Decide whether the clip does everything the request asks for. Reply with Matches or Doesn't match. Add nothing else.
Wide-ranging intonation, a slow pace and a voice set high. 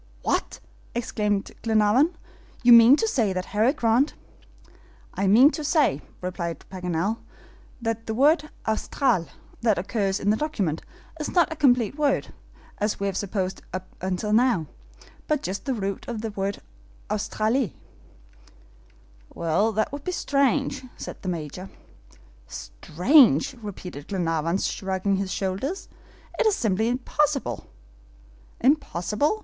Matches